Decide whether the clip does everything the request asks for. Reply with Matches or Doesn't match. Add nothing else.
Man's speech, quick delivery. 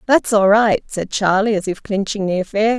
Doesn't match